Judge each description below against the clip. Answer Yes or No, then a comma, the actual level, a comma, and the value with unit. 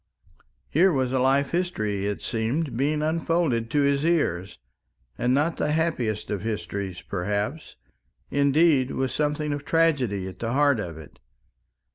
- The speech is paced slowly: No, average, 145 wpm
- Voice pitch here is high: No, low, 135 Hz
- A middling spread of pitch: No, wide, 6.2 semitones